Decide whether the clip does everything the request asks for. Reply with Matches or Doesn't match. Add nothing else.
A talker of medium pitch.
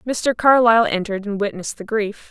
Doesn't match